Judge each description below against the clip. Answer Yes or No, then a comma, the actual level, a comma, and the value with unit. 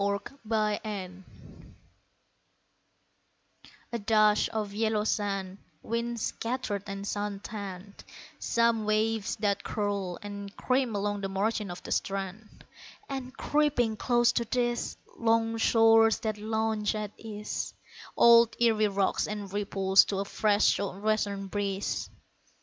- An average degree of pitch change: No, narrow, 2.0 semitones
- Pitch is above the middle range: Yes, high, 210 Hz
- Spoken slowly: Yes, slow, 120 wpm